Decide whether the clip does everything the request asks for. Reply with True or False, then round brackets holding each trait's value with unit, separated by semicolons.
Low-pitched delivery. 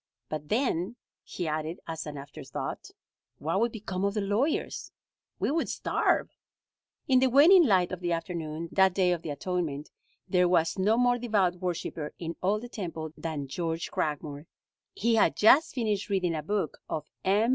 False (180 Hz)